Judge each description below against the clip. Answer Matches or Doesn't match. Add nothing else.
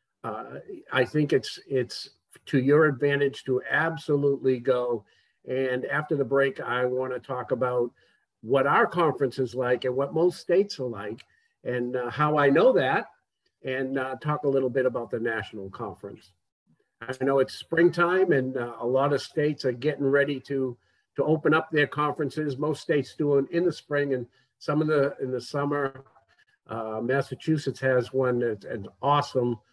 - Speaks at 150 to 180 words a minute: Matches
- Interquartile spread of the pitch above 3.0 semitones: Doesn't match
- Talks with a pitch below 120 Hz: Doesn't match